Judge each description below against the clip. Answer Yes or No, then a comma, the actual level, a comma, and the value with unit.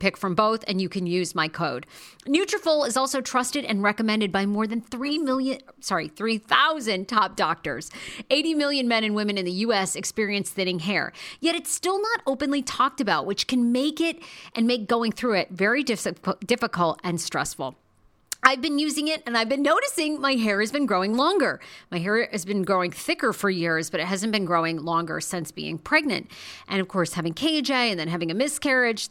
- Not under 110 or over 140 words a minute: No, average, 200 wpm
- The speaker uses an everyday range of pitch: No, wide, 6.2 semitones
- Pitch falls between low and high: No, high, 225 Hz